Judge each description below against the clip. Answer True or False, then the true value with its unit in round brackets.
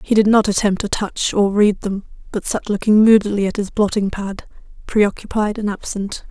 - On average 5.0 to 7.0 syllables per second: True (5.1 syllables/s)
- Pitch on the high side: True (205 Hz)